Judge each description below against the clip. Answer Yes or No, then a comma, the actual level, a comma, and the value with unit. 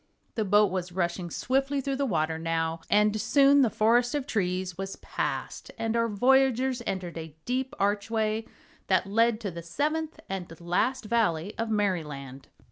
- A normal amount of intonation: No, wide, 5.7 semitones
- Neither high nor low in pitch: No, high, 210 Hz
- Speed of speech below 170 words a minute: Yes, average, 160 wpm